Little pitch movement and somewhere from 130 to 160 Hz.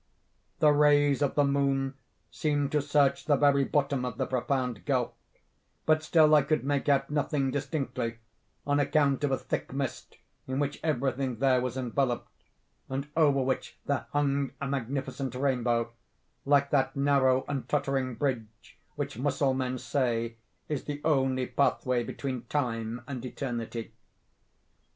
Yes: narrow, 2.0 semitones; low, 135 Hz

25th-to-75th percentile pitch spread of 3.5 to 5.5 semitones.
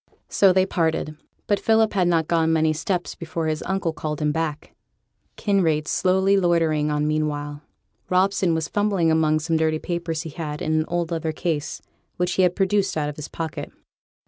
No: average, 2.9 semitones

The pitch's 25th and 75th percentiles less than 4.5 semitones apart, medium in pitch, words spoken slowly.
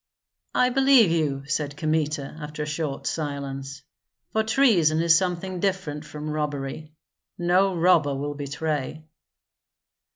Yes: average, 3.5 semitones; medium, 155 Hz; slow, 120 wpm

